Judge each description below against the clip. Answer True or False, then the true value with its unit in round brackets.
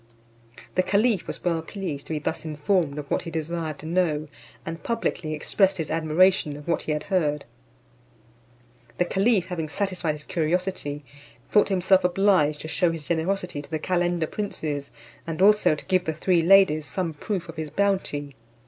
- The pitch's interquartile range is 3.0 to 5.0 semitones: True (3.6 semitones)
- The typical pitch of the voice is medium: True (165 Hz)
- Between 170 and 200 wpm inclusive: True (175 wpm)